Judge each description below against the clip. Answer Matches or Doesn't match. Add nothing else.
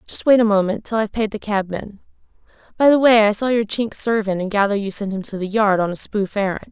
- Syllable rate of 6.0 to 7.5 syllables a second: Matches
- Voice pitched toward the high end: Matches